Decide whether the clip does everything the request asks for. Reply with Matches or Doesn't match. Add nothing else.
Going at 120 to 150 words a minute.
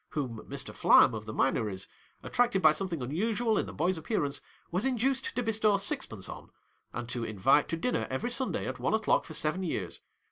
Doesn't match